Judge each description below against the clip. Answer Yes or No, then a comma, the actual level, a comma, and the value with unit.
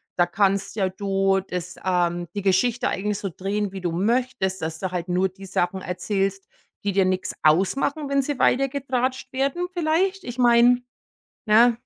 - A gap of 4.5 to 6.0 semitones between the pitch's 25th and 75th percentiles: Yes, average, 5.1 semitones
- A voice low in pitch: No, high, 200 Hz